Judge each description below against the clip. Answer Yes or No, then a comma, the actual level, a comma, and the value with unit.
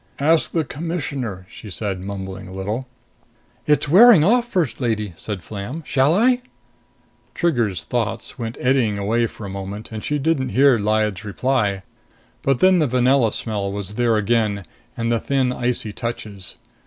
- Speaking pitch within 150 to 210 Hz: No, low, 115 Hz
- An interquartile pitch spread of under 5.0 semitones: No, average, 5.3 semitones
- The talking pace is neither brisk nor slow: Yes, average, 155 wpm